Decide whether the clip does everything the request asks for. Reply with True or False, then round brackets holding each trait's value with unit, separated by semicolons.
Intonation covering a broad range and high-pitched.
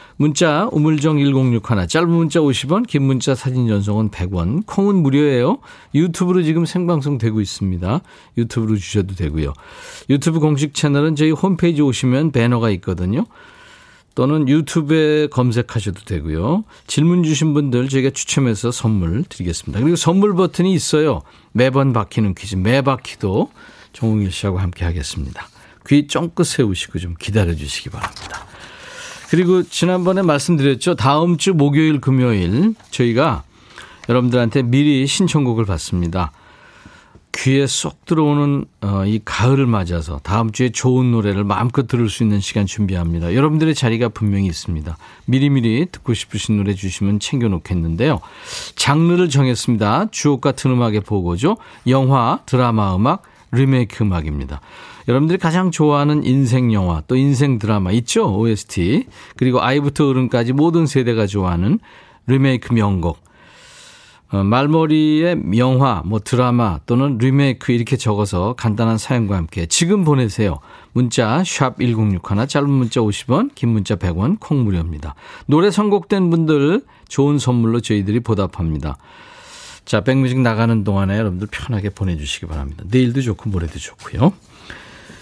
False (6.2 semitones; 125 Hz)